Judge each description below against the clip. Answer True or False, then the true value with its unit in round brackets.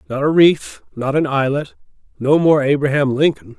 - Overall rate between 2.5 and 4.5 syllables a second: False (4.9 syllables/s)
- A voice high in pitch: False (140 Hz)